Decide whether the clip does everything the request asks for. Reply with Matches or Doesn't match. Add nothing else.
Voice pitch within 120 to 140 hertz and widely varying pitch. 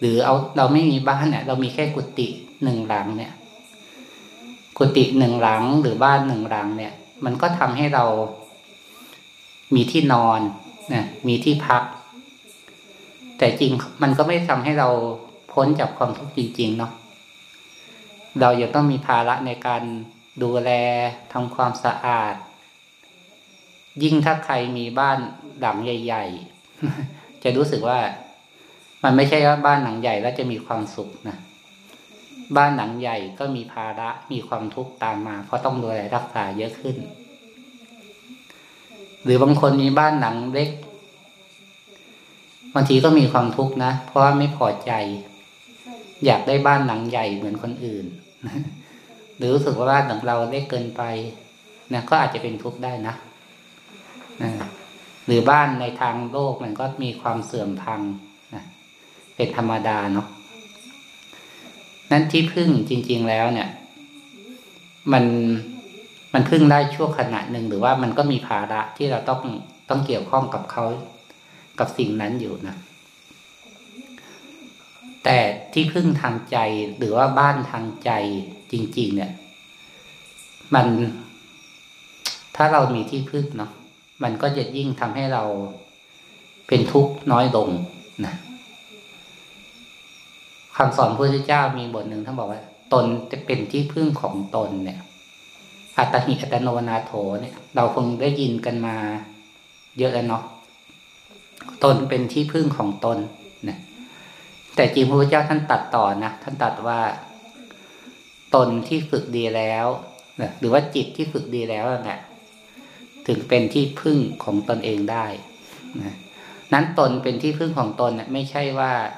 Doesn't match